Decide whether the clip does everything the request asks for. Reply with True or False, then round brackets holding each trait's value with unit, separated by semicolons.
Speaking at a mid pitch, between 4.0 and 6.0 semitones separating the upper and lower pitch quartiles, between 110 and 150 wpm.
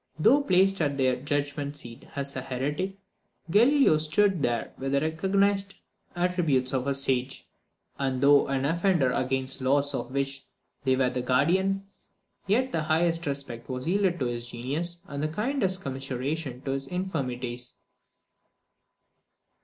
True (145 Hz; 5.3 semitones; 145 wpm)